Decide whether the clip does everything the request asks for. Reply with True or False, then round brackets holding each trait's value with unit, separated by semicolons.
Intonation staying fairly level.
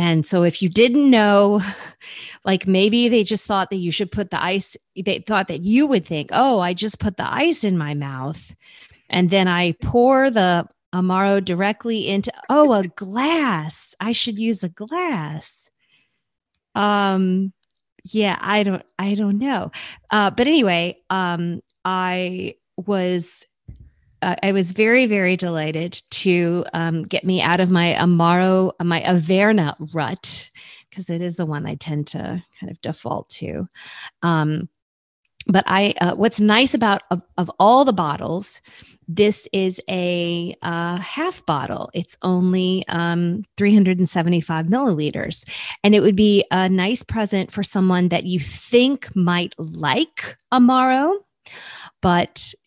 False (3.3 semitones)